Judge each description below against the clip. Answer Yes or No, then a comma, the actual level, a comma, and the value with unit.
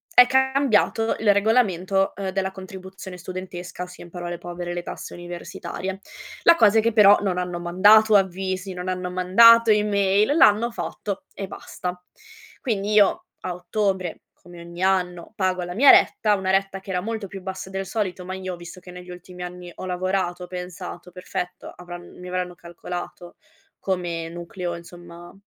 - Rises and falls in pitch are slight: Yes, narrow, 2.1 semitones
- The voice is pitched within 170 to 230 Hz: Yes, medium, 185 Hz